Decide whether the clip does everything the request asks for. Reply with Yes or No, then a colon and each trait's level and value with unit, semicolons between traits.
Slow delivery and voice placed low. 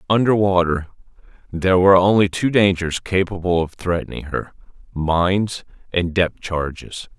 Yes: slow, 115 wpm; very low, 90 Hz